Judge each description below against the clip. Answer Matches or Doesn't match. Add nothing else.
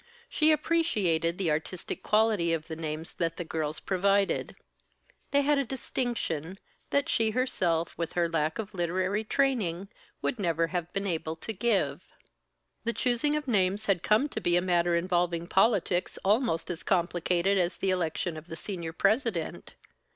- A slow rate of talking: Doesn't match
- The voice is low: Doesn't match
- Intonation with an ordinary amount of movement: Matches